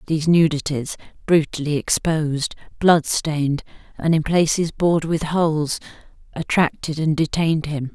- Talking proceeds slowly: Yes, slow, 115 wpm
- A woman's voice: Yes, female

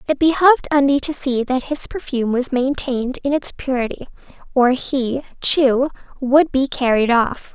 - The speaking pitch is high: Yes, very high, 265 Hz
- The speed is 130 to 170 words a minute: Yes, average, 160 wpm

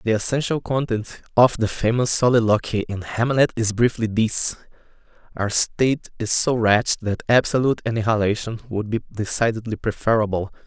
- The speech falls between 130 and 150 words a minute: Yes, slow, 135 wpm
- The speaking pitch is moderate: No, low, 115 Hz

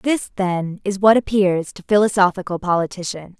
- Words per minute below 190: Yes, average, 140 wpm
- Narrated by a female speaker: Yes, female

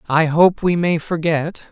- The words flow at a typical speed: Yes, average, 175 wpm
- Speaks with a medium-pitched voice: Yes, medium, 165 Hz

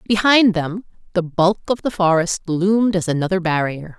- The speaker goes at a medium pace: Yes, average, 165 wpm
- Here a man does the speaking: No, female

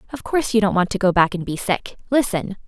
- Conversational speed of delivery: No, fast, 270 wpm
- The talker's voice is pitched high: Yes, high, 205 Hz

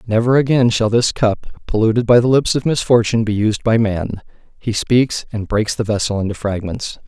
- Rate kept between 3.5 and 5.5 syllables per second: Yes, 5.4 syllables/s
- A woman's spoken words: No, male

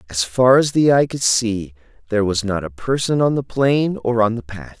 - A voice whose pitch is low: Yes, low, 115 Hz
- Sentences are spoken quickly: Yes, fast, 240 wpm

